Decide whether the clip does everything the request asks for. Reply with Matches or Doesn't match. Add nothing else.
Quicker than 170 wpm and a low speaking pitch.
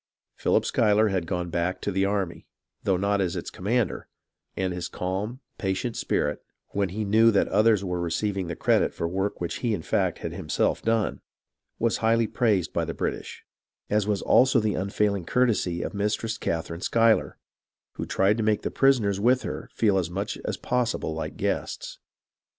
Matches